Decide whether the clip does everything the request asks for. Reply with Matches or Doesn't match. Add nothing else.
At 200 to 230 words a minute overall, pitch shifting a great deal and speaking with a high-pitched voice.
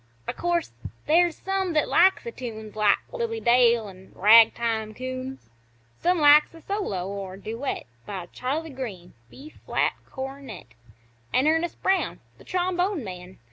Doesn't match